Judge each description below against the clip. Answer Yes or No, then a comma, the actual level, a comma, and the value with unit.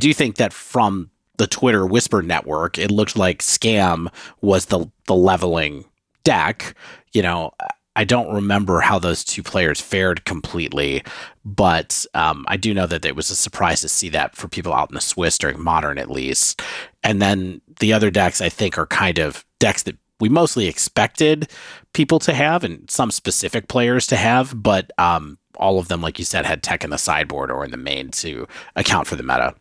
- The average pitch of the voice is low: Yes, very low, 95 Hz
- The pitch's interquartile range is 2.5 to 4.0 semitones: No, average, 4.8 semitones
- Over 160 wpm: Yes, average, 200 wpm